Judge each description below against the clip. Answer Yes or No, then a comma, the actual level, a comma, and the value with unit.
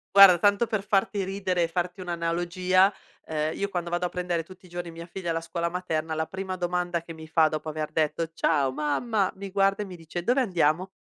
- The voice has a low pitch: No, medium, 175 Hz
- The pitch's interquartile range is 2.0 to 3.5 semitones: Yes, narrow, 2.6 semitones